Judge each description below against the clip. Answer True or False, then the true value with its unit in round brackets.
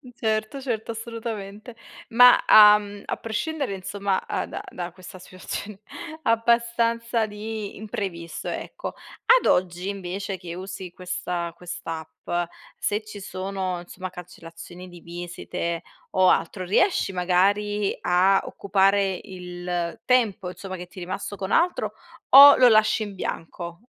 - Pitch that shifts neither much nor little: True (3.3 semitones)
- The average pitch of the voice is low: False (195 Hz)